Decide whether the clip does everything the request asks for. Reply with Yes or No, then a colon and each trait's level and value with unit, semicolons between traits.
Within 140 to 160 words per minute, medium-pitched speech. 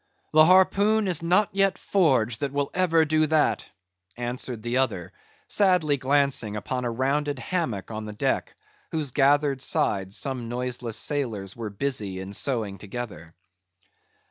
No: average, 145 wpm; low, 130 Hz